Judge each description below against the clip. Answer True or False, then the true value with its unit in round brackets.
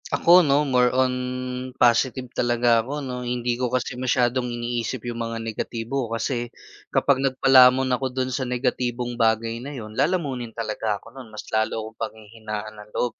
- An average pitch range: False (2.2 semitones)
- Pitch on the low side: True (120 Hz)